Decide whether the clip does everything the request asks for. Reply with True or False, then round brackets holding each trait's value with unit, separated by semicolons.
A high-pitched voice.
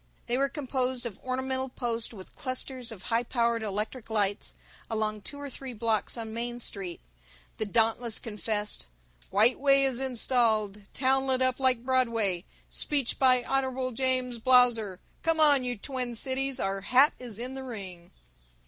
True (245 Hz)